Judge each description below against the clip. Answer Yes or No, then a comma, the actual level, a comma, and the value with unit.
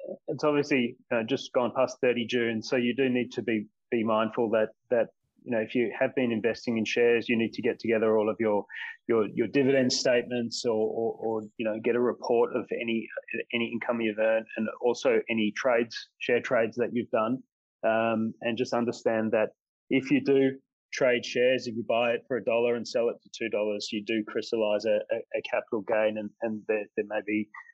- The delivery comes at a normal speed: No, fast, 210 wpm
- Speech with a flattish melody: Yes, narrow, 2.2 semitones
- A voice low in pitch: Yes, low, 115 Hz